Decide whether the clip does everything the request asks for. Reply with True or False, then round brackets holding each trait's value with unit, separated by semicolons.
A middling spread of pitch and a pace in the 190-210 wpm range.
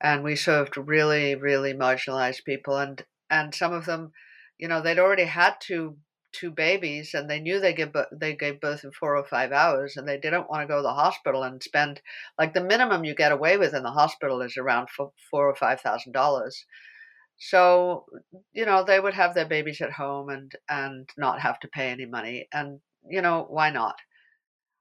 True (3.7 semitones; 200 wpm)